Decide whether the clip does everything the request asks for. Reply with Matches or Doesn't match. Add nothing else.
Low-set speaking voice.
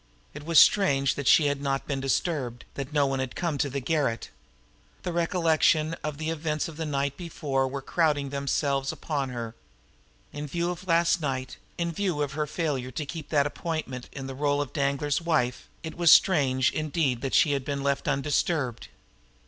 Doesn't match